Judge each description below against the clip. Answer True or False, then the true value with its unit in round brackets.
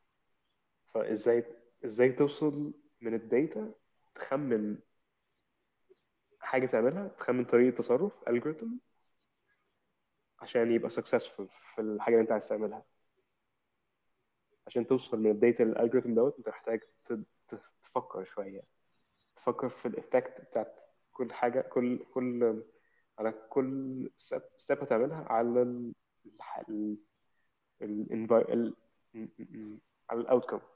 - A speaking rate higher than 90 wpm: True (110 wpm)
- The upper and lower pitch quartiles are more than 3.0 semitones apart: False (2.7 semitones)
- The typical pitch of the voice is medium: False (120 Hz)